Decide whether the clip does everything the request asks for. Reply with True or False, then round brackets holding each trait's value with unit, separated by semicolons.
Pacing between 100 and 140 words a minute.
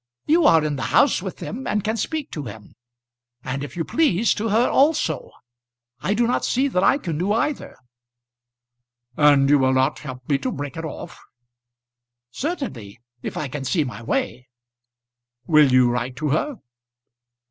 False (170 wpm)